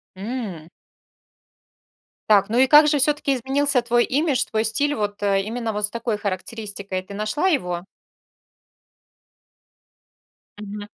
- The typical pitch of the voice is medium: No, high, 220 Hz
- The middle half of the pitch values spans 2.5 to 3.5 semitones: No, average, 4.8 semitones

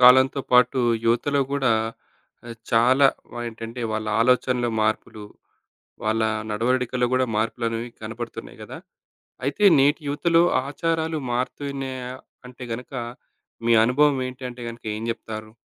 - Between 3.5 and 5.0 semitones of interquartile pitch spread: No, average, 2.9 semitones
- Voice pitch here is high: No, low, 125 Hz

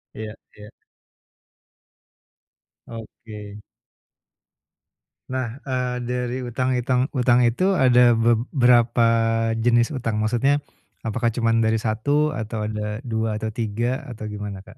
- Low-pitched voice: Yes, low, 120 Hz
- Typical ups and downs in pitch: No, narrow, 2.3 semitones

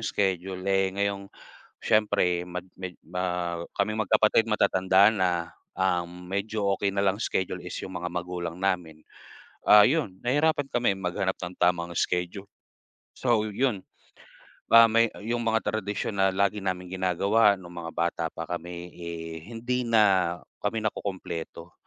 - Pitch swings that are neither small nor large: Yes, average, 3.3 semitones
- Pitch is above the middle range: No, very low, 95 Hz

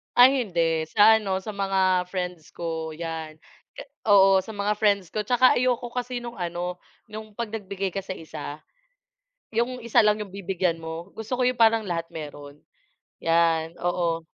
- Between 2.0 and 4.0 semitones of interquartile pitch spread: No, average, 4.7 semitones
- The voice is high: Yes, high, 195 Hz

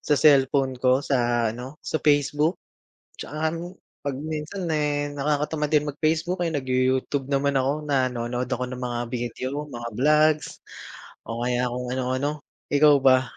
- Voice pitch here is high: No, medium, 140 Hz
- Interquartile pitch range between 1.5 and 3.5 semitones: Yes, average, 3.0 semitones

